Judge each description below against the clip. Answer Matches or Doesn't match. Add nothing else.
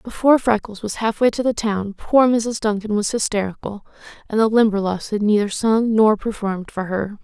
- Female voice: Matches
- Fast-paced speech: Doesn't match